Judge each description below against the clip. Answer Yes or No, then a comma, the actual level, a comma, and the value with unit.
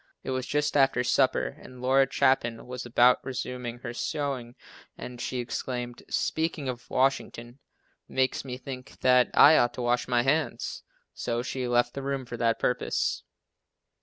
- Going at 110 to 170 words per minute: Yes, average, 160 wpm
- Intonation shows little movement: Yes, narrow, 1.8 semitones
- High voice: No, low, 125 Hz